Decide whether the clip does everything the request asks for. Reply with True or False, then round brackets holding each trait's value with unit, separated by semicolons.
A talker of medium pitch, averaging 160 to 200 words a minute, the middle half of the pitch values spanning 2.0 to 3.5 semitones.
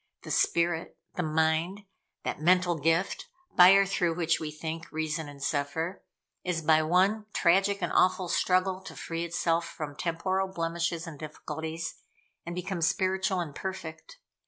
False (170 Hz; 150 wpm; 2.6 semitones)